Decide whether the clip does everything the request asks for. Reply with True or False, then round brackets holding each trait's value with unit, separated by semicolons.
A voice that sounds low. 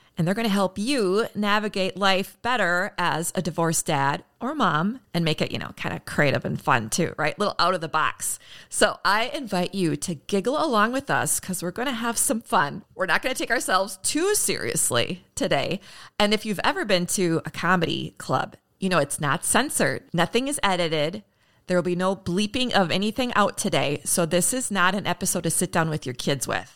False (185 Hz)